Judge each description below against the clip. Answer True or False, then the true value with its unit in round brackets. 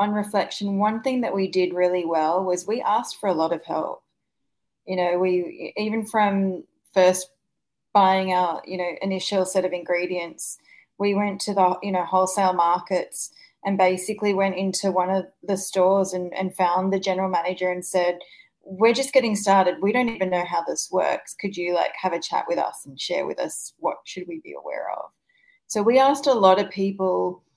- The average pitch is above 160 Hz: True (190 Hz)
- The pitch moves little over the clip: True (1.9 semitones)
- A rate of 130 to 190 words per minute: False (200 wpm)